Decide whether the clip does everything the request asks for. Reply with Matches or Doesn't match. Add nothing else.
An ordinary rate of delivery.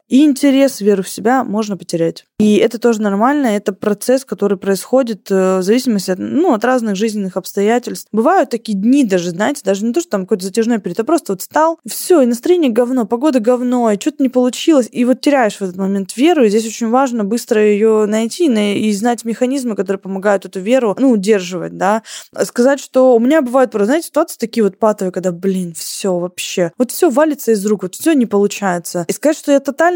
Doesn't match